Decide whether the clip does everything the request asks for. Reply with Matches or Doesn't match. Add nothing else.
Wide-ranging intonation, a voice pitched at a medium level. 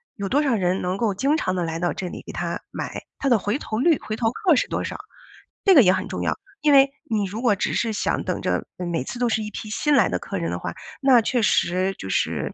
Doesn't match